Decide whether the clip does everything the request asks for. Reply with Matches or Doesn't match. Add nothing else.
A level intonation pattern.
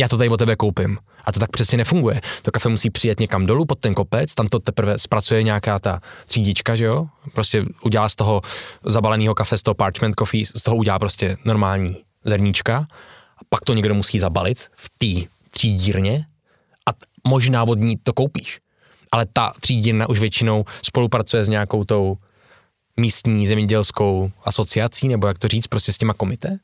Matches